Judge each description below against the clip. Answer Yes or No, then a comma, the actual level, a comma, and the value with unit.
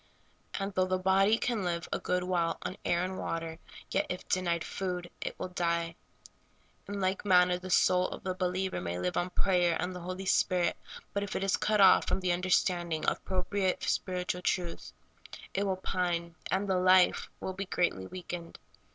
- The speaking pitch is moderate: Yes, medium, 180 Hz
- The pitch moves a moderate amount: No, narrow, 1.4 semitones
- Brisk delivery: No, average, 185 wpm